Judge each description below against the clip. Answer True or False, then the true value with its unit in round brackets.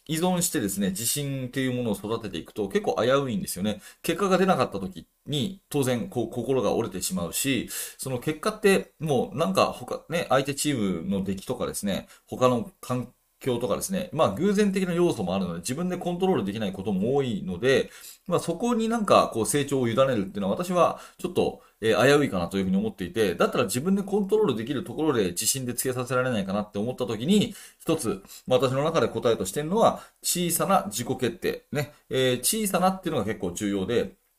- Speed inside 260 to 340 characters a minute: False (435 characters per minute)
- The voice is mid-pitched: True (145 Hz)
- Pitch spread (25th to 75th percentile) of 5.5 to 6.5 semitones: False (7.6 semitones)